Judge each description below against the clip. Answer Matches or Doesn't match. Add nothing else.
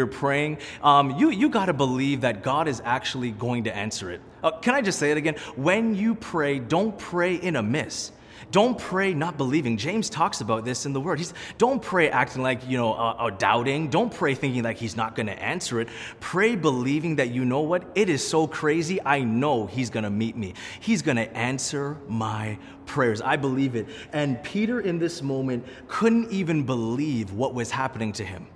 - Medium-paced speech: Doesn't match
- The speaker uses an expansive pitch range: Matches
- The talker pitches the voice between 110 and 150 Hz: Matches